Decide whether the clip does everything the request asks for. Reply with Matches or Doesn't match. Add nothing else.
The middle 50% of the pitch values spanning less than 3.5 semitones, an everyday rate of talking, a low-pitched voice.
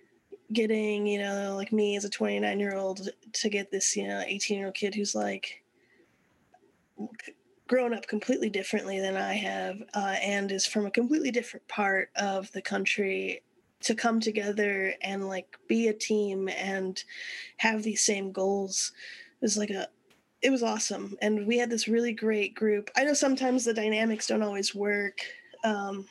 Doesn't match